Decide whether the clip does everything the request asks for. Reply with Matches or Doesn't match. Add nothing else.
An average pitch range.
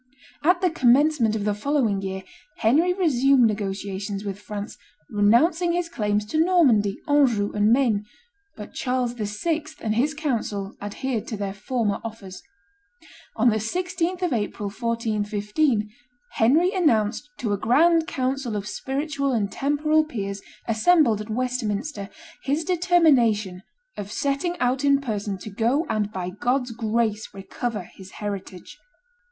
Doesn't match